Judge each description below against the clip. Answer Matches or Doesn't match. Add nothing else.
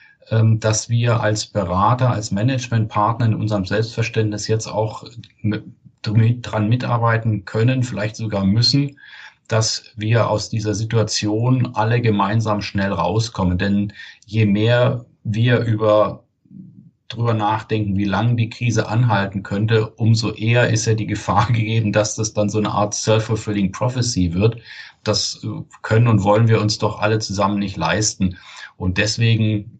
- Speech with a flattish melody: Matches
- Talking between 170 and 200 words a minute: Doesn't match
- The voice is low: Matches